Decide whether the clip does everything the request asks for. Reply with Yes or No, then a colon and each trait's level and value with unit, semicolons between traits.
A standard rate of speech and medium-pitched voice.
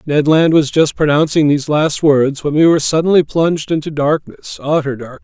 Yes: average, 195 wpm; medium, 150 Hz